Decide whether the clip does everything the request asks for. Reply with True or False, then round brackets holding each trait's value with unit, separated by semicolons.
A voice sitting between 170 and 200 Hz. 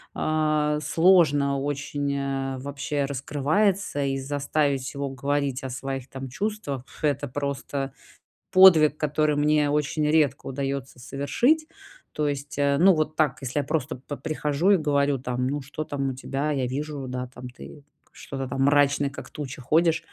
False (140 Hz)